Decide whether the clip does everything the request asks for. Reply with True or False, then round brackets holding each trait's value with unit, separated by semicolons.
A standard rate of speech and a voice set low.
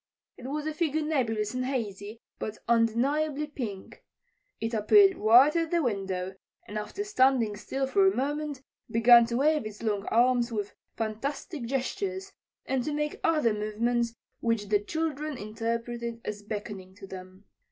False (150 wpm; 235 Hz)